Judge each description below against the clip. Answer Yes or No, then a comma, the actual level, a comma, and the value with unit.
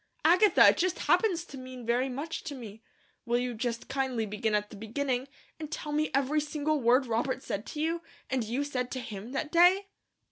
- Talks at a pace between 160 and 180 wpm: No, fast, 205 wpm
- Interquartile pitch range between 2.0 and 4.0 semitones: No, average, 4.5 semitones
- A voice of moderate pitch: No, very high, 265 Hz